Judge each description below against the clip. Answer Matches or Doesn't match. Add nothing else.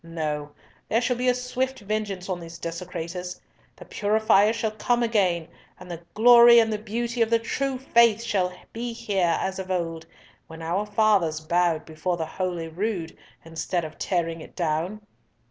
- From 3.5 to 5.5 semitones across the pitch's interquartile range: Matches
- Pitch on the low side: Doesn't match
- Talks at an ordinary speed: Matches